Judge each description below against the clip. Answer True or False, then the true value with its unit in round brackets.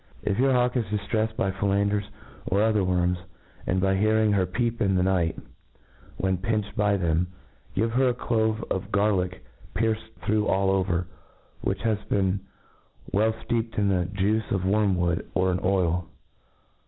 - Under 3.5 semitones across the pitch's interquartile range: True (2.8 semitones)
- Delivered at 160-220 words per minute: True (165 wpm)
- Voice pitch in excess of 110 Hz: False (100 Hz)